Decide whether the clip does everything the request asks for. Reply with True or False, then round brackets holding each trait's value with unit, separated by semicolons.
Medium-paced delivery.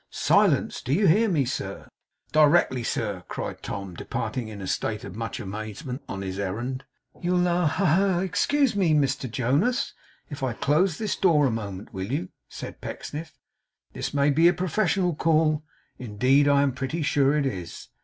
True (175 wpm)